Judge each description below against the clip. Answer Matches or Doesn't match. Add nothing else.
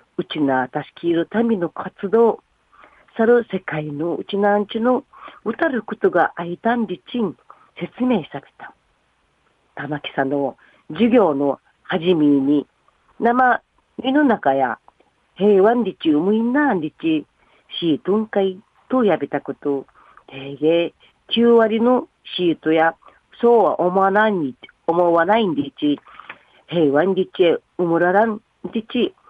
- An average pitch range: Doesn't match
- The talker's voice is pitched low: Doesn't match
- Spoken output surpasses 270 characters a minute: Doesn't match